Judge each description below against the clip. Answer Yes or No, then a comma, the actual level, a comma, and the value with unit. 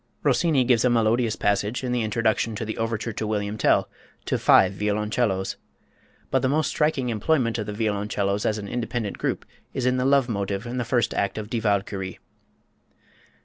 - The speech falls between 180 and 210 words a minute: Yes, average, 185 wpm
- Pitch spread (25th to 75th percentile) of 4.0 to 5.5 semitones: No, average, 3.1 semitones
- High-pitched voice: No, low, 110 Hz